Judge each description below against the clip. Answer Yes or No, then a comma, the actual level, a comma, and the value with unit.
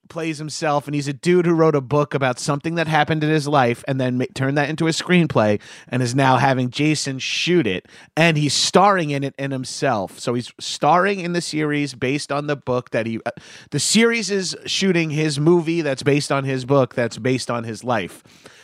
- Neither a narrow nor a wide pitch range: Yes, average, 4.0 semitones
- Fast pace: Yes, fast, 220 wpm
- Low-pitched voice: No, medium, 145 Hz